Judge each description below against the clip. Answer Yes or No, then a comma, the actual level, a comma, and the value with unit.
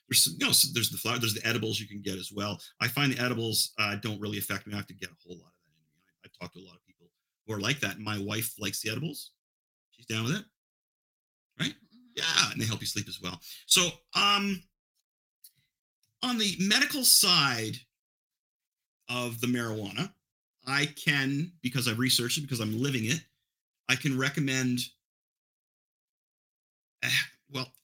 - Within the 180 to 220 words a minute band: Yes, average, 190 wpm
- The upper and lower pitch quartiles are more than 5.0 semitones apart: Yes, wide, 5.5 semitones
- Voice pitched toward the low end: Yes, low, 120 Hz